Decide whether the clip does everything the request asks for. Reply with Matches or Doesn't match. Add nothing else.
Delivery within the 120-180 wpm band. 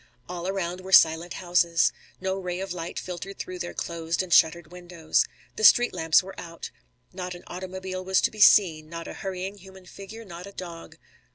Doesn't match